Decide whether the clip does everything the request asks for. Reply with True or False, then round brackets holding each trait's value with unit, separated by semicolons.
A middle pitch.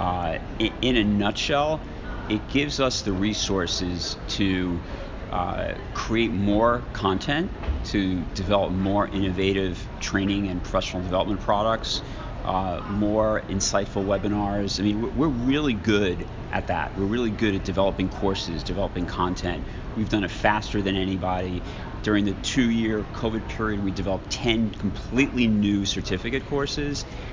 False (100 Hz)